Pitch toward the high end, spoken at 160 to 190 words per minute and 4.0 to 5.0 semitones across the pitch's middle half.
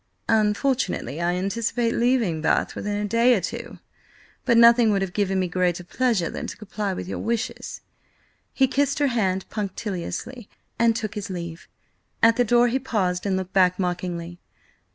Yes: high, 205 Hz; average, 170 wpm; average, 4.4 semitones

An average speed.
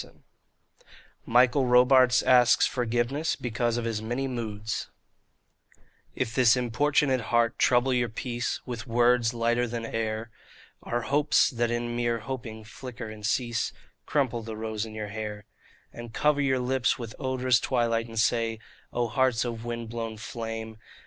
Yes: average, 155 wpm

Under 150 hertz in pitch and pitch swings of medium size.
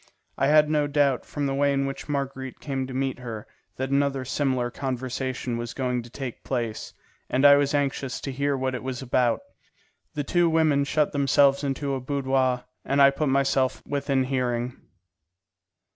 No: low, 135 Hz; narrow, 1.7 semitones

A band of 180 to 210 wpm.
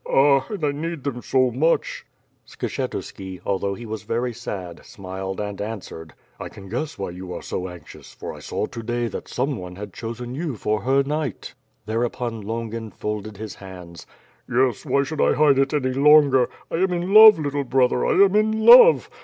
Yes: average, 195 wpm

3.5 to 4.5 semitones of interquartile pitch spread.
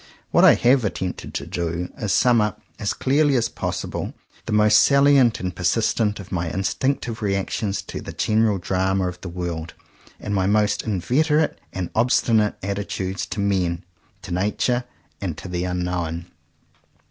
Yes: average, 3.9 semitones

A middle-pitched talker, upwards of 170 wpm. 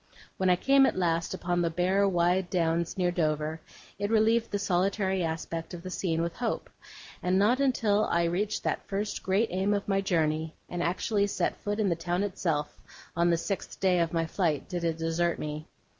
Yes: medium, 180 Hz; average, 200 wpm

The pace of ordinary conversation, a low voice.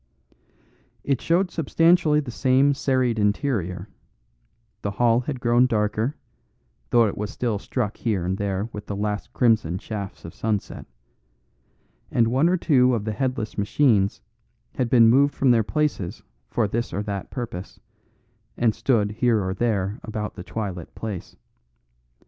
Yes: average, 150 wpm; low, 115 Hz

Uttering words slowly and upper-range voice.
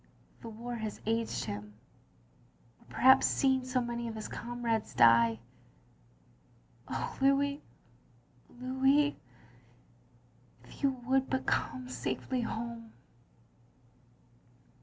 Yes: slow, 105 wpm; high, 235 Hz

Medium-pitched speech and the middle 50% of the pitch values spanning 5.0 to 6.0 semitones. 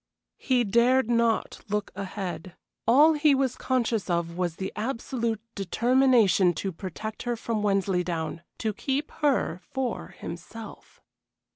No: high, 220 Hz; average, 5.3 semitones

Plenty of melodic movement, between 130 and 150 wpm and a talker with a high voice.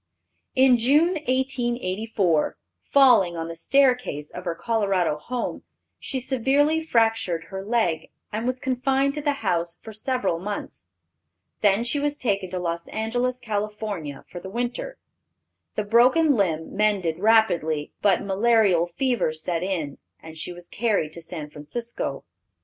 Yes: wide, 6.5 semitones; average, 140 wpm; high, 210 Hz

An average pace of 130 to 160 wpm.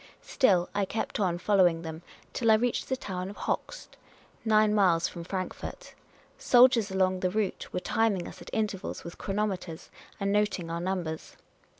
No: average, 170 wpm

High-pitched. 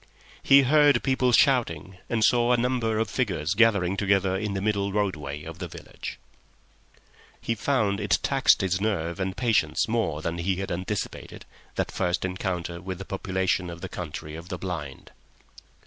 No: very low, 95 Hz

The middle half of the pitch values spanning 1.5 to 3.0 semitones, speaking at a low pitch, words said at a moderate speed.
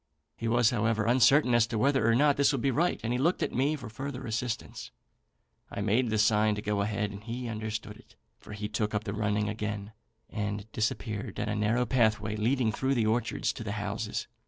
No: average, 2.7 semitones; low, 110 Hz; fast, 220 wpm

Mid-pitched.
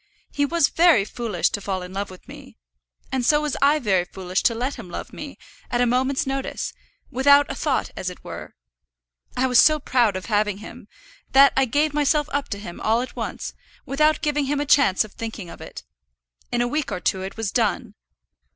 No: high, 245 Hz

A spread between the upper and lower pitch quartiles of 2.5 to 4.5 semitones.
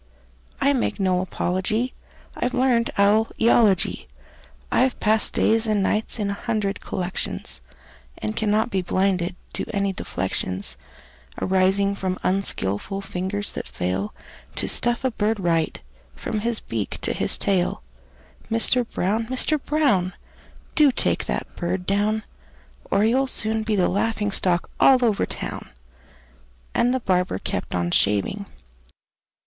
Yes: average, 3.6 semitones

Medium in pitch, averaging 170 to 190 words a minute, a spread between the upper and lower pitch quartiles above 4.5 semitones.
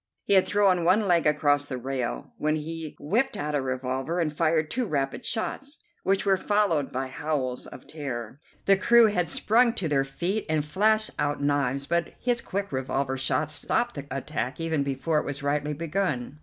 Yes: medium, 150 Hz; average, 185 wpm; wide, 5.6 semitones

